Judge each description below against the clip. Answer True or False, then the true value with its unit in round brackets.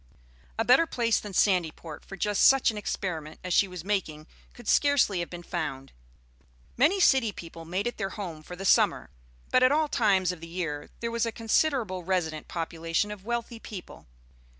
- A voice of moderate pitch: False (195 Hz)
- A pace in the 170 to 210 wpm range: True (185 wpm)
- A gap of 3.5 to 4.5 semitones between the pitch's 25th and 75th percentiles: False (5.6 semitones)